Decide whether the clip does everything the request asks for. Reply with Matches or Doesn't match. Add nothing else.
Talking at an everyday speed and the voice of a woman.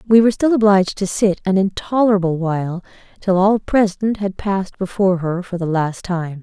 Matches